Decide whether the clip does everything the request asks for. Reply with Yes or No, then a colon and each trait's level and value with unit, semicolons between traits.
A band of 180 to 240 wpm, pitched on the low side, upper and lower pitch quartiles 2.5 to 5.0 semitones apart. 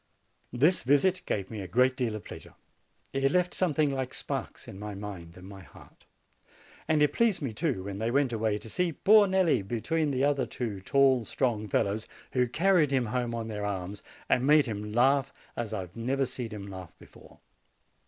No: average, 195 wpm; low, 125 Hz; wide, 5.4 semitones